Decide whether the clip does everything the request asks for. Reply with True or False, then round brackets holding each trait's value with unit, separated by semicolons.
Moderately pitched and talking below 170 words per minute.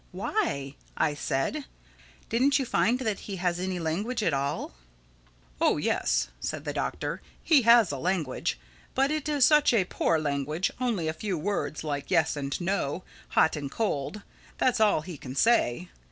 True (180 Hz; 160 wpm)